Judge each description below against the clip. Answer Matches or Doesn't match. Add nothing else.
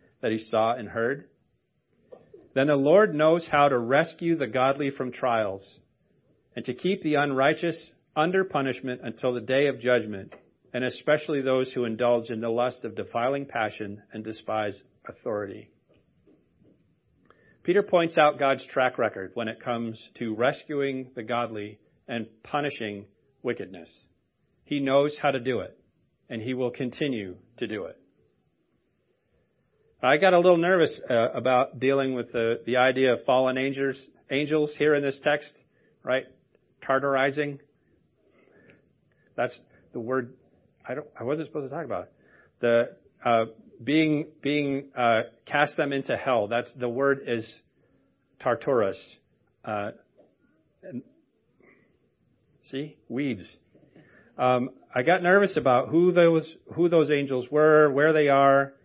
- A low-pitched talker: Matches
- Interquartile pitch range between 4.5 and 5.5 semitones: Doesn't match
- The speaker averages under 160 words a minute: Matches